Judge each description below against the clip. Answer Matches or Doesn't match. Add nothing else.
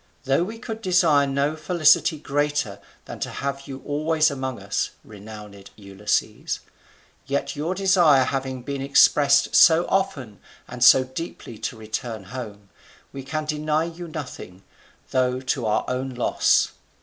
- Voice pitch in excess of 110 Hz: Matches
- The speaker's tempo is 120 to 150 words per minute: Matches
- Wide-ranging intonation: Doesn't match